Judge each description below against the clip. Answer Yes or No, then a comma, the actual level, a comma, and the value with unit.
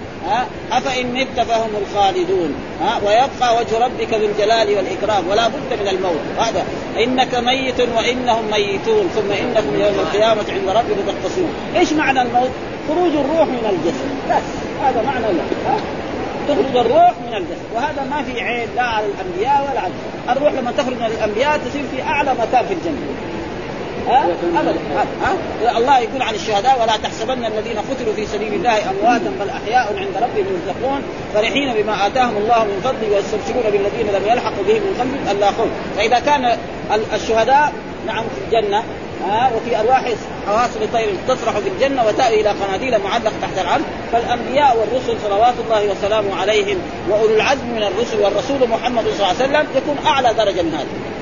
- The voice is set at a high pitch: Yes, high, 240 Hz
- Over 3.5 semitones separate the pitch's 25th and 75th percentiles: Yes, average, 4.9 semitones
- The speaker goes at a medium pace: No, fast, 160 wpm